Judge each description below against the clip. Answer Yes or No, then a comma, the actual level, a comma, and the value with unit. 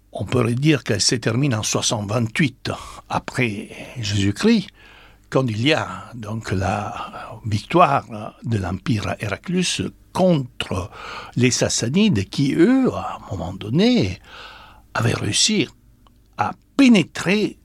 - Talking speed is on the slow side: Yes, slow, 110 wpm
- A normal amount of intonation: No, wide, 6.7 semitones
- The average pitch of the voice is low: Yes, low, 120 Hz